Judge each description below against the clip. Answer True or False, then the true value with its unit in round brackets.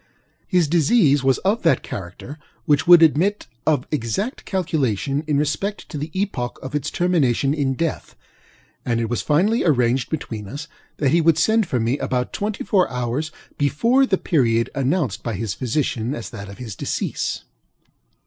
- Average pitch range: False (5.7 semitones)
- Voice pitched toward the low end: False (145 Hz)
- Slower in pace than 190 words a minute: True (170 wpm)